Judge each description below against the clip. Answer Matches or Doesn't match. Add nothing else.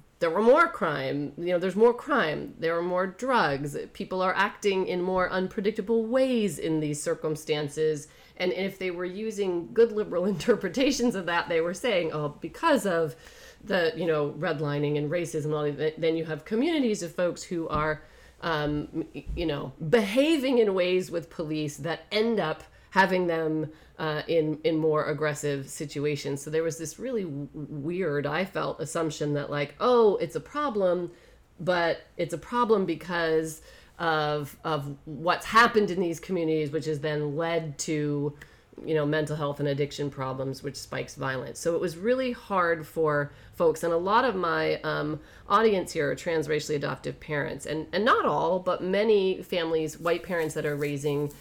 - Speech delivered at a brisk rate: Doesn't match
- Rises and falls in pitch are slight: Doesn't match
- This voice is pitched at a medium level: Matches